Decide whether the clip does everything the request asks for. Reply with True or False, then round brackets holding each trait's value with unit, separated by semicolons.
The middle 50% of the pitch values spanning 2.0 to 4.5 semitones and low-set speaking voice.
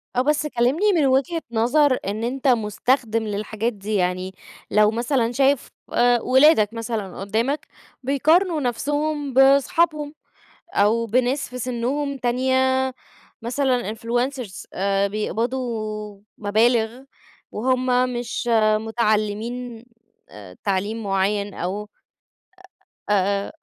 False (3.9 semitones; 240 Hz)